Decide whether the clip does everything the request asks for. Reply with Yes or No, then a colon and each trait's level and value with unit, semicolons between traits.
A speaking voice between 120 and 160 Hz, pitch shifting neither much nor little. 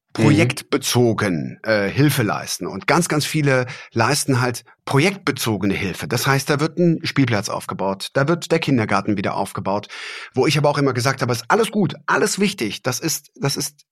Yes: medium, 140 Hz; average, 4.5 semitones